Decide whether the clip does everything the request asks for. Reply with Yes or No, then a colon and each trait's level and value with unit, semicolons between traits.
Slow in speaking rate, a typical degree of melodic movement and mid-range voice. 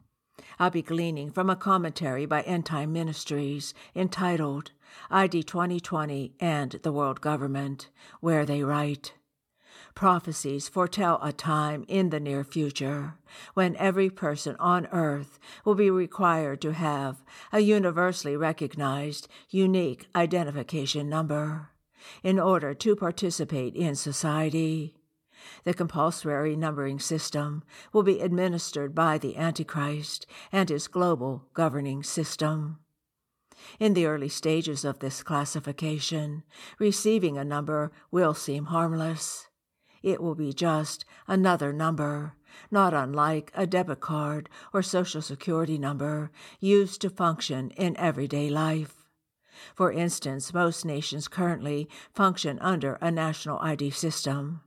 Yes: slow, 120 wpm; average, 3.2 semitones; medium, 155 Hz